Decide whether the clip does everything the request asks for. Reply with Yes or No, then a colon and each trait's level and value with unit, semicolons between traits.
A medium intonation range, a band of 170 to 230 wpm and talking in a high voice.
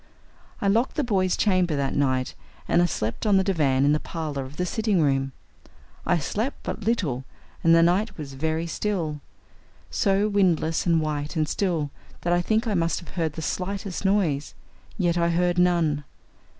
No: average, 4.4 semitones; average, 180 wpm; medium, 170 Hz